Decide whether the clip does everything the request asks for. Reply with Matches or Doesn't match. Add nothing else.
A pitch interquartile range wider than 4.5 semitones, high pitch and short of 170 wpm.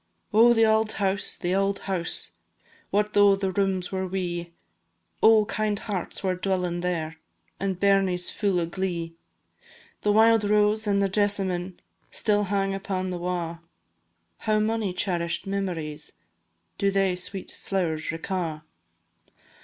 Doesn't match